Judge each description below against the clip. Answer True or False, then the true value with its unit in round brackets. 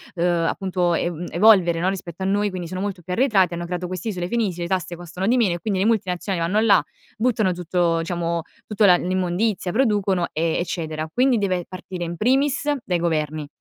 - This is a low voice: False (180 Hz)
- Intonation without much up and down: False (3.1 semitones)